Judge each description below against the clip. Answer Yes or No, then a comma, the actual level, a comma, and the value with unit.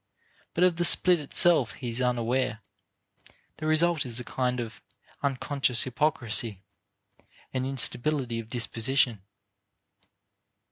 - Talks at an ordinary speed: No, slow, 110 wpm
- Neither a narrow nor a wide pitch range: Yes, average, 4.1 semitones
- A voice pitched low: Yes, low, 130 Hz